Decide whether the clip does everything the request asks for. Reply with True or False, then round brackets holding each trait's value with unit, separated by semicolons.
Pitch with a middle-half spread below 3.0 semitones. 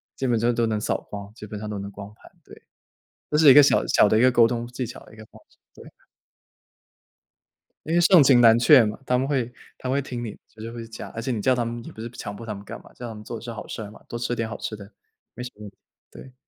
True (2.6 semitones)